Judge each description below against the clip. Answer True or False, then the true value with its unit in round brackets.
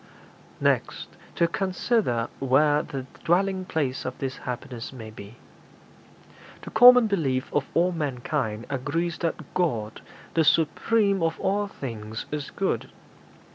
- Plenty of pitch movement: True (6.2 semitones)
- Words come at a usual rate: False (125 wpm)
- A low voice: False (150 Hz)